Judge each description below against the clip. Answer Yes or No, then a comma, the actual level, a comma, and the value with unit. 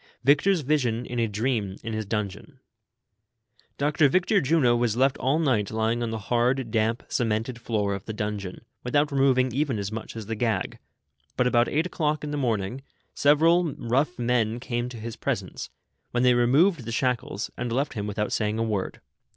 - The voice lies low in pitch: Yes, low, 120 Hz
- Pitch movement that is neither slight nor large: Yes, average, 3.9 semitones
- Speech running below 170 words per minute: No, average, 190 wpm